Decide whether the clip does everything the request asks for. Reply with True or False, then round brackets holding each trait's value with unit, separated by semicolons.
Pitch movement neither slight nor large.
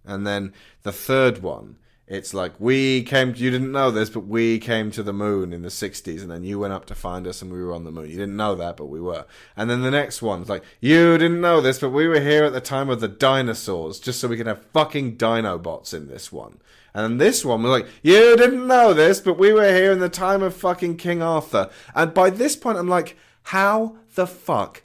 False (8.8 semitones)